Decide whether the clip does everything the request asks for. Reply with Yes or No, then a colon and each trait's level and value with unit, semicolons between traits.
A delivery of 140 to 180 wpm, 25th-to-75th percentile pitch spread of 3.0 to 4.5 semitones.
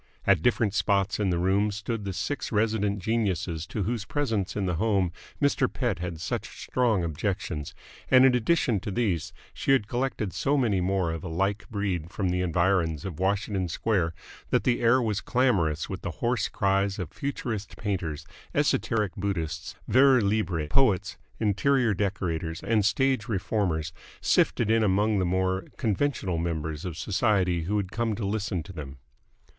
Yes: average, 165 wpm; average, 3.9 semitones